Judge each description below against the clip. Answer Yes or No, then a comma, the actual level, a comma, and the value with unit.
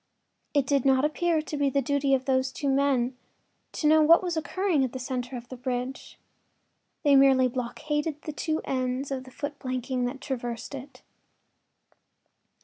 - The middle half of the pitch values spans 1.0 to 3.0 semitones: Yes, narrow, 2.5 semitones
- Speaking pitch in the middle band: No, very high, 270 Hz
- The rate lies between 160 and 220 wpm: Yes, average, 170 wpm